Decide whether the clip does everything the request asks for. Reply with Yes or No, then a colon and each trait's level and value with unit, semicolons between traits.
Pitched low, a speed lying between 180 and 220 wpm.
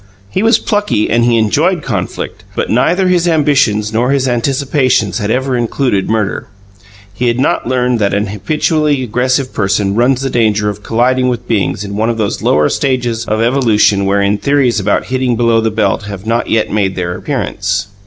Yes: low, 115 Hz; average, 185 wpm